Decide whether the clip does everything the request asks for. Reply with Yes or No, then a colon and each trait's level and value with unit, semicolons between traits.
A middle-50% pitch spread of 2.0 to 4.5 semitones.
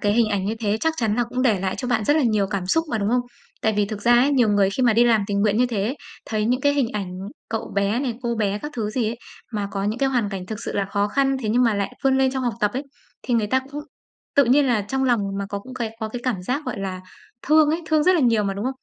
Yes: average, 4.0 semitones